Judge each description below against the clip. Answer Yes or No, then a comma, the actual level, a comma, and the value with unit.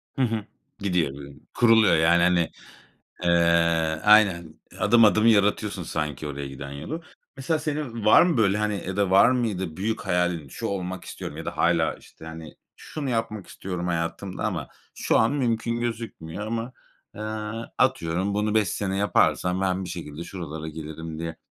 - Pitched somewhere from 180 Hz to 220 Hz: No, very low, 95 Hz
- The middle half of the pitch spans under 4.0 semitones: No, average, 5.1 semitones